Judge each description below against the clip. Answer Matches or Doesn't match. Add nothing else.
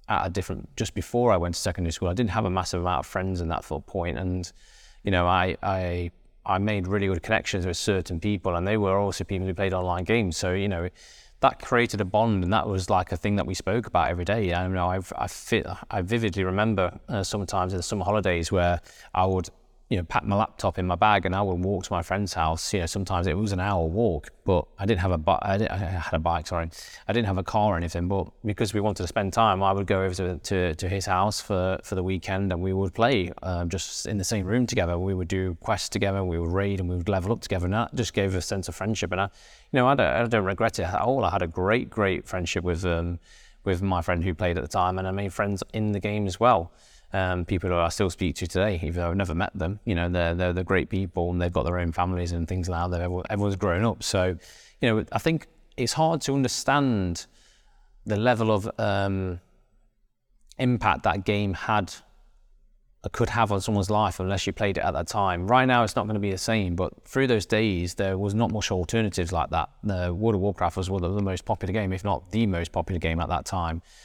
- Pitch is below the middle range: Matches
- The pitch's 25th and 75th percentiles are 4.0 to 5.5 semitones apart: Doesn't match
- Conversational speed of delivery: Doesn't match